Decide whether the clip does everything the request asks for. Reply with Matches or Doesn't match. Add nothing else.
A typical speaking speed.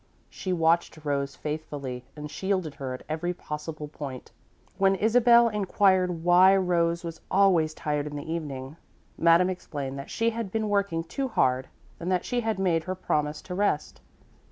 Matches